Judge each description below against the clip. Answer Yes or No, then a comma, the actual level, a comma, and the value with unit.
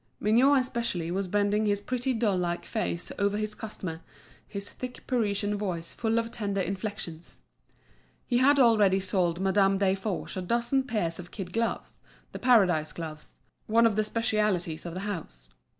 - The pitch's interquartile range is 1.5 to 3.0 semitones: No, average, 4.1 semitones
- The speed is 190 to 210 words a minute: No, average, 160 wpm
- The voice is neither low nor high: No, high, 205 Hz